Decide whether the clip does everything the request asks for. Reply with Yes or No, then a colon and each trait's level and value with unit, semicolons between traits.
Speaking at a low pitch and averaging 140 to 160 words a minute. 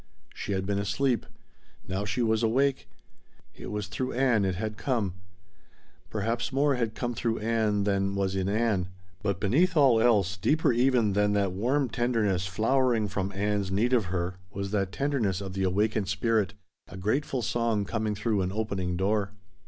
No: low, 105 Hz; average, 170 wpm